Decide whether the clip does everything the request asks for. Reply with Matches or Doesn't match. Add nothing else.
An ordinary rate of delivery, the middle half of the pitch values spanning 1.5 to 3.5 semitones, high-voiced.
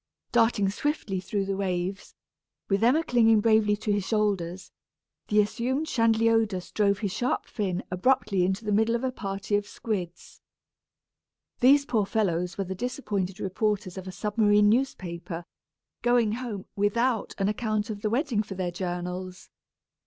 Matches